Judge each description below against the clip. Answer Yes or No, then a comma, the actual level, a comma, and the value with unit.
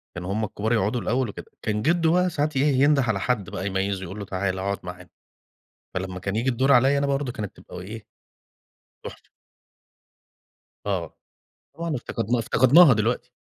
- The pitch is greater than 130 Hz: No, low, 110 Hz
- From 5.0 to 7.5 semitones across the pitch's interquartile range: Yes, wide, 5.6 semitones